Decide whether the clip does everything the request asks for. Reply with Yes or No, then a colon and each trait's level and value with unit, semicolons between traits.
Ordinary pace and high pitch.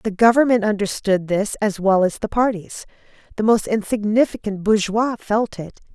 Yes: average, 150 wpm; high, 210 Hz